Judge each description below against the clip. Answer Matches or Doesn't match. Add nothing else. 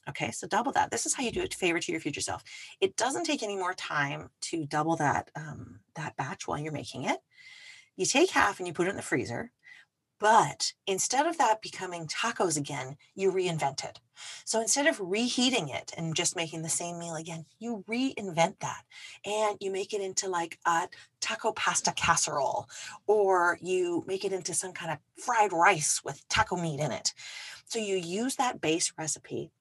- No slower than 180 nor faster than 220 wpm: Matches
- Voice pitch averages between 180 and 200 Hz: Matches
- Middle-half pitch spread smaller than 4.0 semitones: Doesn't match